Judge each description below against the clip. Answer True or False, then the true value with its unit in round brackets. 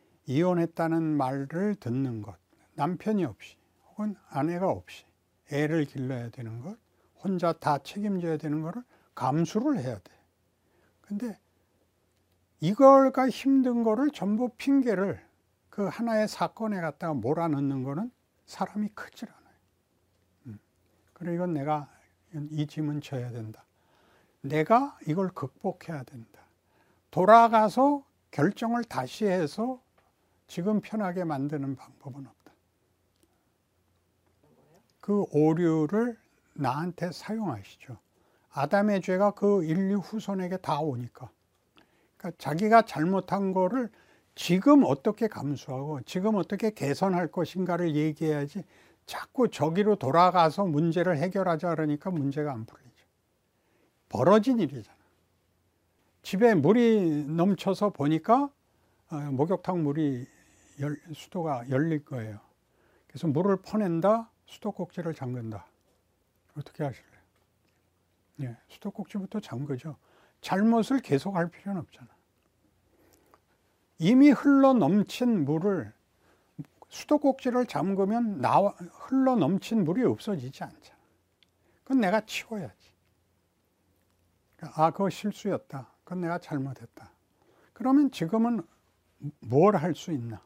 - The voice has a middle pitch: True (160 Hz)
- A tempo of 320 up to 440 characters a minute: False (240 characters per minute)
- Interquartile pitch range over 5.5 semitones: True (8.1 semitones)